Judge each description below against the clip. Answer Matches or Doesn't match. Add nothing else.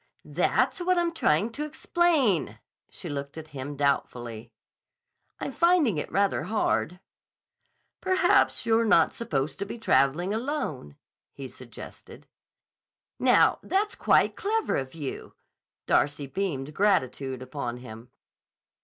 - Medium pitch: Matches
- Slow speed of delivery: Matches